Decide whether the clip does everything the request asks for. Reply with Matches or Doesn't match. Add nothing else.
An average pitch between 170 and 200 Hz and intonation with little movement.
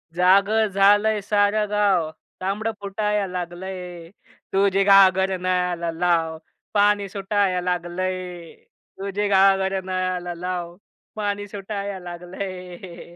Matches